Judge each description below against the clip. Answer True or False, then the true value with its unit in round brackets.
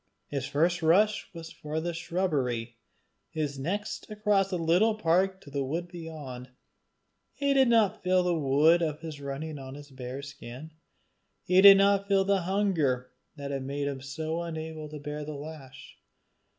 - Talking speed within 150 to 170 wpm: True (165 wpm)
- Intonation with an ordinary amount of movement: True (4.7 semitones)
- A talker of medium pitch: True (160 Hz)